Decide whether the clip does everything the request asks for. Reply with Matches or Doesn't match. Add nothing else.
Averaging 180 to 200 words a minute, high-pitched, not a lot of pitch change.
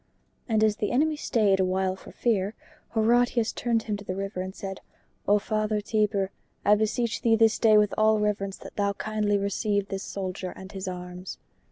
Matches